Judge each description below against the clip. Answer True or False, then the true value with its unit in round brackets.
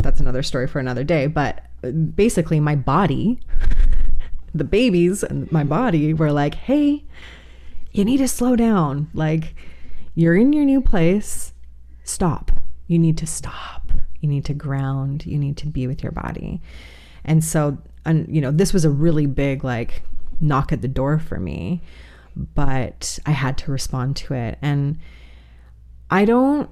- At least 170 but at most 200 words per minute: False (160 wpm)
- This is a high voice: False (140 Hz)